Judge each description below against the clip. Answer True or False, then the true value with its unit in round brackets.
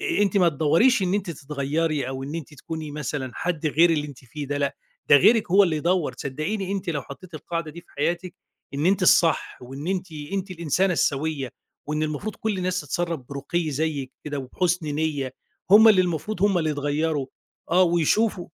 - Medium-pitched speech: True (160 Hz)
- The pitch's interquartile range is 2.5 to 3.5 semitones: False (4.0 semitones)